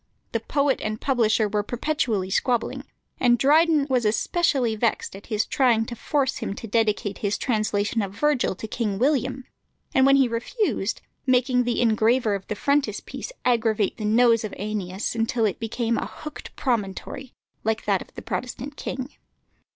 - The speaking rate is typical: Yes, average, 165 wpm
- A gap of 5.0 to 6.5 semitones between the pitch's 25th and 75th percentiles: No, average, 3.5 semitones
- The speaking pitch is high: Yes, high, 230 Hz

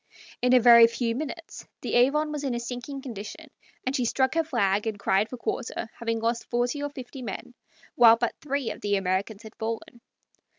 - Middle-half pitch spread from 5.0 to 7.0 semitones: No, average, 3.1 semitones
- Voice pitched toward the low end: No, high, 240 Hz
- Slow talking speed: No, average, 200 wpm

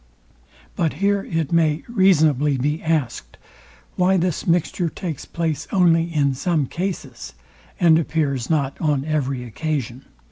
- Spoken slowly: Yes, slow, 130 wpm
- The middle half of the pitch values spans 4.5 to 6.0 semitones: No, average, 3.4 semitones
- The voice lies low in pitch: No, medium, 155 Hz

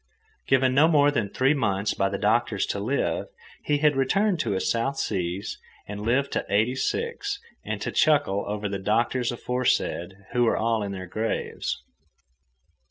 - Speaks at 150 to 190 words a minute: Yes, average, 165 wpm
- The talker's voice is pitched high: No, low, 115 Hz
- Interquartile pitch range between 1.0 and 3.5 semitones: No, average, 5.2 semitones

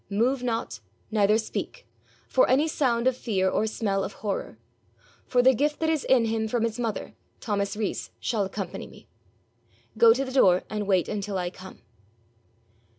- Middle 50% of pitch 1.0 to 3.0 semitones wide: No, average, 3.9 semitones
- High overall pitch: Yes, high, 220 Hz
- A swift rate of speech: No, average, 170 wpm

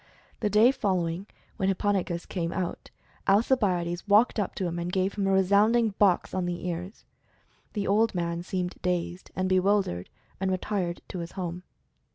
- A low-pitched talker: No, medium, 185 Hz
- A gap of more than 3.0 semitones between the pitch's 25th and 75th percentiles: No, narrow, 2.6 semitones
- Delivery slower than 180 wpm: Yes, average, 165 wpm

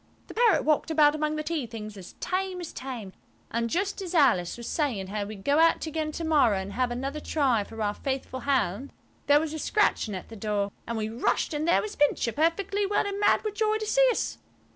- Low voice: No, very high, 290 Hz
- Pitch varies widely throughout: Yes, wide, 7.0 semitones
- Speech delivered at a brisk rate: Yes, fast, 225 wpm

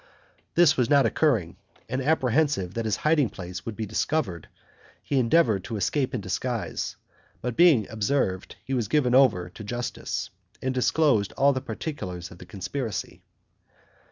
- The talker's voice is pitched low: Yes, low, 120 Hz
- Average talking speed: Yes, average, 150 wpm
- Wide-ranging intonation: Yes, wide, 6.1 semitones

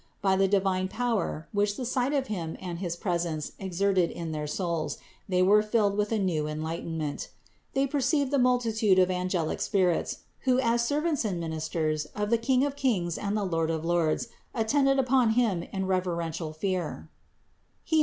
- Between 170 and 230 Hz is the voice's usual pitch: Yes, high, 190 Hz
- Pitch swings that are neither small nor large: No, wide, 5.8 semitones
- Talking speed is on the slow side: No, average, 170 wpm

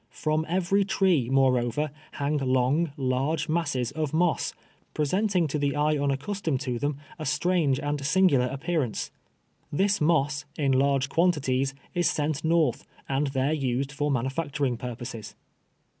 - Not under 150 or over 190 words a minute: No, average, 140 wpm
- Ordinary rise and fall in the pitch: Yes, average, 3.2 semitones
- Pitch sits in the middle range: Yes, medium, 145 Hz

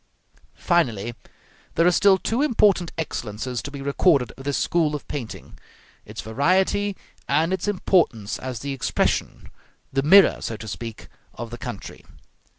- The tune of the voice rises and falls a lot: Yes, wide, 7.4 semitones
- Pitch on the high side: No, medium, 145 Hz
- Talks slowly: No, average, 150 wpm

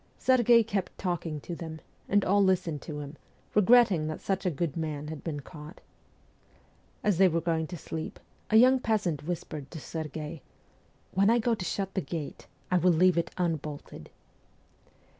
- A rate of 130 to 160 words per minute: No, average, 170 wpm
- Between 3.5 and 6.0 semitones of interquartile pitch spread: Yes, average, 4.0 semitones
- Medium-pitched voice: Yes, medium, 170 Hz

